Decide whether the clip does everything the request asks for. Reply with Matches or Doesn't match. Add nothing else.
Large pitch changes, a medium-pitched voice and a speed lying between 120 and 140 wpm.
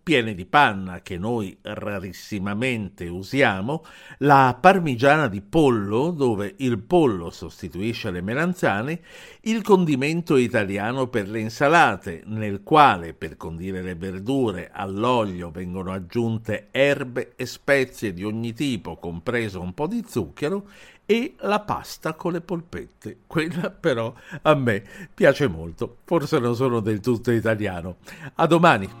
Doesn't match